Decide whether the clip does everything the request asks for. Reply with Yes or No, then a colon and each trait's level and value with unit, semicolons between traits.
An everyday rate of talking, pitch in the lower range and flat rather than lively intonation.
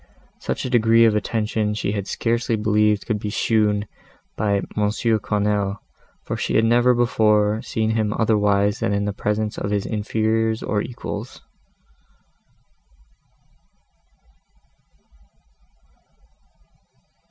No: slow, 110 wpm; low, 105 Hz; narrow, 1.4 semitones